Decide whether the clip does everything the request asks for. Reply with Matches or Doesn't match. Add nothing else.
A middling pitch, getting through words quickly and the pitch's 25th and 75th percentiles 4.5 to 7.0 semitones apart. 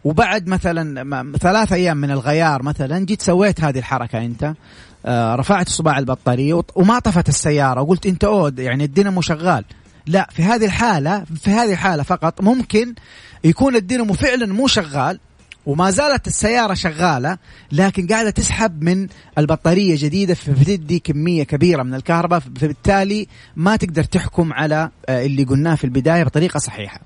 Matches